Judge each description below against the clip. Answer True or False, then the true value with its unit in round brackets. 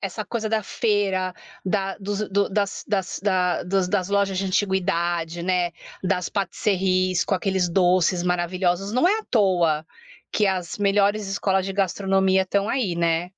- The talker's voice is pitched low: False (190 Hz)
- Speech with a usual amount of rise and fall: False (1.9 semitones)